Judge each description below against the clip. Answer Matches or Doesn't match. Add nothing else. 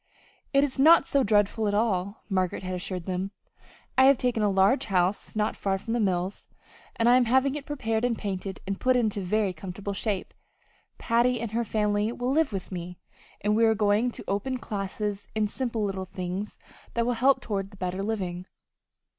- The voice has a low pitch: Doesn't match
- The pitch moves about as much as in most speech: Matches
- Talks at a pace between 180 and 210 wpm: Matches